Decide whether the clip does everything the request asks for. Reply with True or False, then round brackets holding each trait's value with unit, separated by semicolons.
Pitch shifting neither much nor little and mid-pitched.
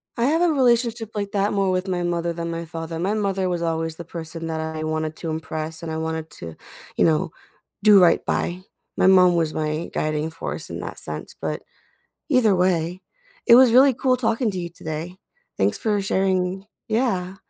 True (4.2 semitones; 180 Hz)